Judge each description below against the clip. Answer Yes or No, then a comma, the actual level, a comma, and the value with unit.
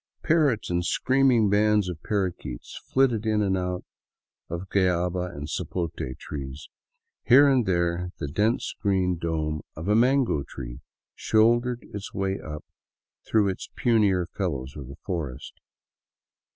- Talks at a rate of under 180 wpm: Yes, slow, 135 wpm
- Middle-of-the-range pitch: No, very low, 95 Hz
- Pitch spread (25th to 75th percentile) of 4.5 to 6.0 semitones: Yes, average, 4.8 semitones